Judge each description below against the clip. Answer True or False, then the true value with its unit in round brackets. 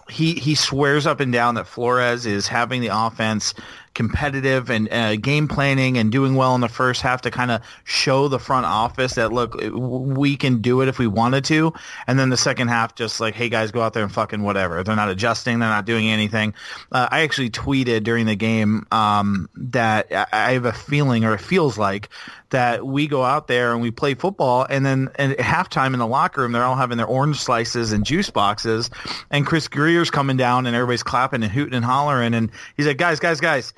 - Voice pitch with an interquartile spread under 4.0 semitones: True (3.3 semitones)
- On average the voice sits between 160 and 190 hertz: False (125 Hz)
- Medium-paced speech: False (220 wpm)